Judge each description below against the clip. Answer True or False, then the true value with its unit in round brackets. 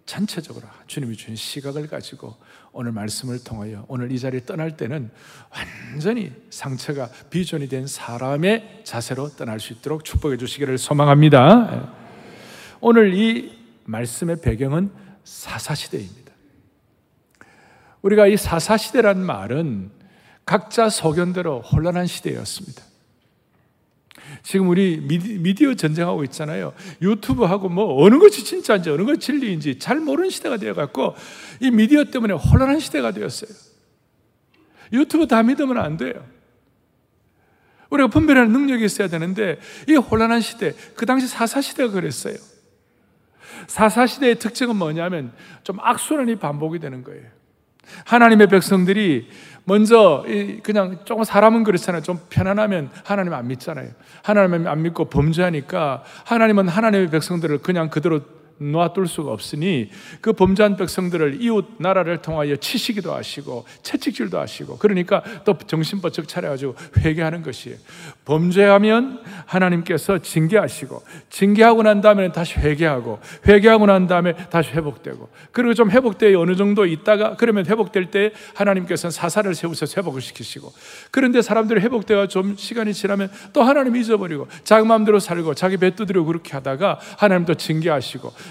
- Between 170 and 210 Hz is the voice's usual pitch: True (185 Hz)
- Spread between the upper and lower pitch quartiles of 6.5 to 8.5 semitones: False (5.7 semitones)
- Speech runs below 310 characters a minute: False (340 characters per minute)